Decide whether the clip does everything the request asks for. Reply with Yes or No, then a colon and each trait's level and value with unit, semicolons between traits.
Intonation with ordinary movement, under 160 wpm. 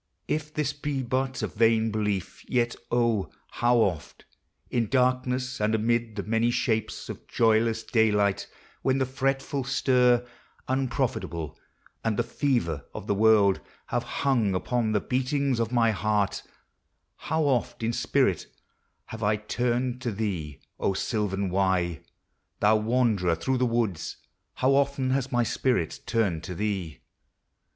Yes: average, 3.6 semitones; average, 140 wpm